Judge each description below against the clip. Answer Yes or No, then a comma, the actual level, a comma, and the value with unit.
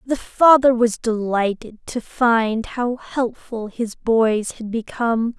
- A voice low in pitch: No, high, 230 Hz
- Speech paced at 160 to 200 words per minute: No, slow, 135 wpm